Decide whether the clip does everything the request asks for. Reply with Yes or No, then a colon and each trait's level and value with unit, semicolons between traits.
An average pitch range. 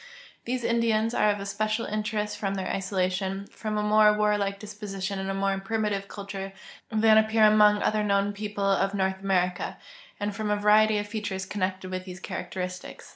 No: narrow, 1.6 semitones